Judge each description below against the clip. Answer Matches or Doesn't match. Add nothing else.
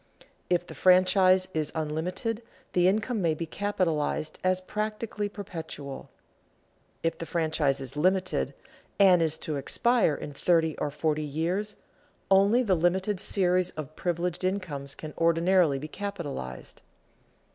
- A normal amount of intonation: Matches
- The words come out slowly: Matches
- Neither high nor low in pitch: Matches